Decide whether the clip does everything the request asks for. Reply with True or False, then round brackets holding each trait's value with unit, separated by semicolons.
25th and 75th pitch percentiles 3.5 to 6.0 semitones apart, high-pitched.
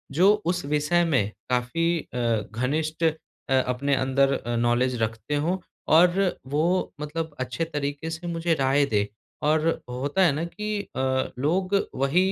False (4.4 semitones; 150 Hz)